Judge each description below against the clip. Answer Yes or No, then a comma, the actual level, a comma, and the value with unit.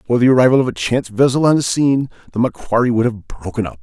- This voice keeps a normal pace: No, fast, 250 wpm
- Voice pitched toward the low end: Yes, low, 120 Hz